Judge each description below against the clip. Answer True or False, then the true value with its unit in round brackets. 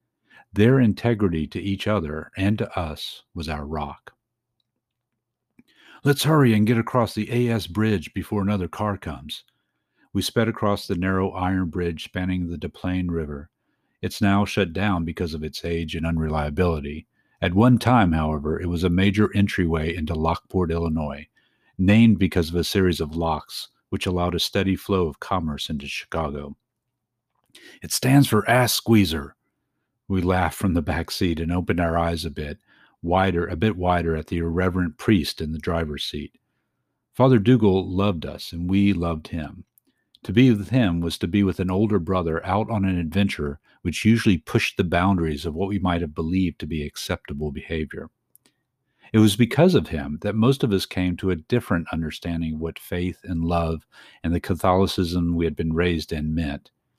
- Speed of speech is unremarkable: True (175 wpm)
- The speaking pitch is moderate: False (90 Hz)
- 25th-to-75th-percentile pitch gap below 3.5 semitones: False (4.2 semitones)